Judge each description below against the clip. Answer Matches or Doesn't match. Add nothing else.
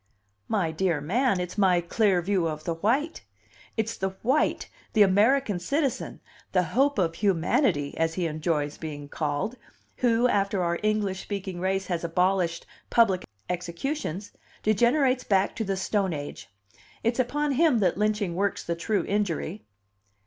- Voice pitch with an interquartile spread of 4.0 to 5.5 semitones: Matches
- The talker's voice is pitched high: Matches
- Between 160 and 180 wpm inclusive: Doesn't match